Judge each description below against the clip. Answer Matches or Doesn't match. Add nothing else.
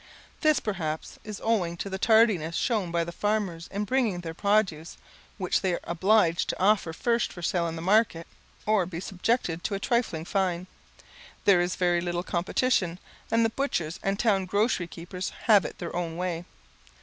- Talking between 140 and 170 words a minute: Doesn't match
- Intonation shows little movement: Doesn't match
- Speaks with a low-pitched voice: Doesn't match